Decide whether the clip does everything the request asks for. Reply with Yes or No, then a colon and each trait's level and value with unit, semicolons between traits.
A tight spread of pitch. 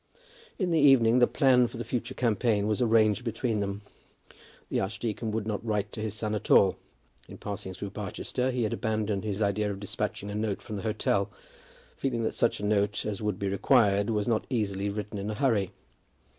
Yes: narrow, 2.2 semitones